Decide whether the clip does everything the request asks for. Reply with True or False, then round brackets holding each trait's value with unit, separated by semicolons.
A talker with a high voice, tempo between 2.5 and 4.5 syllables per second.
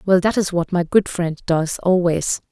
False (180 Hz; 4.4 syllables/s)